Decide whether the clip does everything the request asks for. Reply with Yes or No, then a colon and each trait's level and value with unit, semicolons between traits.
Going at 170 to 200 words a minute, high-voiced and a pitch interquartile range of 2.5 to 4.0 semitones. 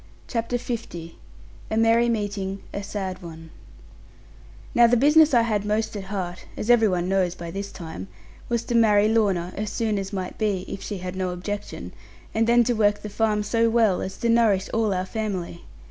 Yes: average, 190 wpm; high, 210 Hz; average, 3.3 semitones